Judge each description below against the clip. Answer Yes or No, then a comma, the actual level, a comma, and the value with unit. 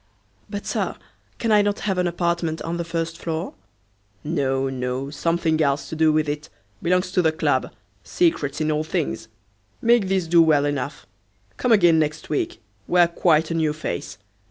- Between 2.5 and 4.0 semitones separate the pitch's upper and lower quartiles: Yes, average, 2.8 semitones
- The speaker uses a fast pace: No, average, 175 wpm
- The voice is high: No, medium, 160 Hz